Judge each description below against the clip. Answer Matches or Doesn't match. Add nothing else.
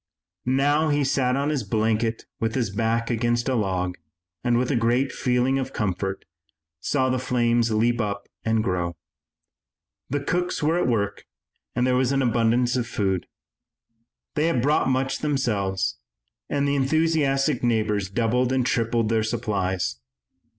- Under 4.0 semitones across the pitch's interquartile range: Matches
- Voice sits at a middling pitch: Doesn't match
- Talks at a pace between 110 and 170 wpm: Matches